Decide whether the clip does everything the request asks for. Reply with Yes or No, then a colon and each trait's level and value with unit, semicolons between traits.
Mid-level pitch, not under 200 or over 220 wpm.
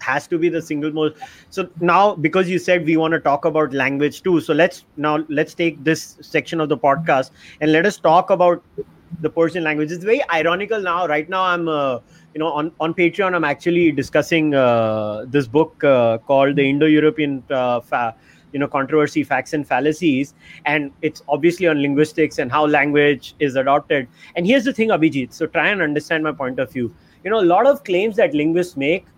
Yes: medium, 155 Hz; fast, 205 wpm